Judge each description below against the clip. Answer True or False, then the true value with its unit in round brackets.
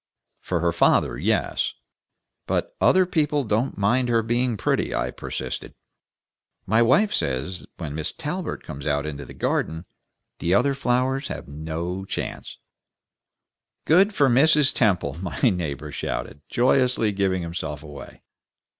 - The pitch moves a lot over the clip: True (9.0 semitones)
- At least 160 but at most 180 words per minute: False (135 wpm)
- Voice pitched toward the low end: True (100 Hz)